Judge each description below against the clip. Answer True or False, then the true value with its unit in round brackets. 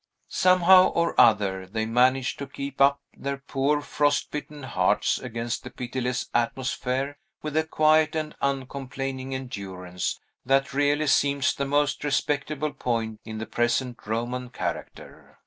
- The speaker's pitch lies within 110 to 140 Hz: True (135 Hz)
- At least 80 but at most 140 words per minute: True (135 wpm)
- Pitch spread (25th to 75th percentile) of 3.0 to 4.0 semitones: True (3.3 semitones)